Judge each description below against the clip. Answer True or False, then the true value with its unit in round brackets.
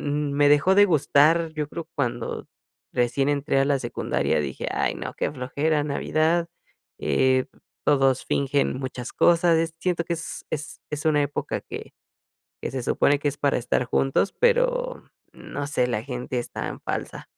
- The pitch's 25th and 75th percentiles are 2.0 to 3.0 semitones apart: False (3.5 semitones)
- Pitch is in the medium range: True (145 Hz)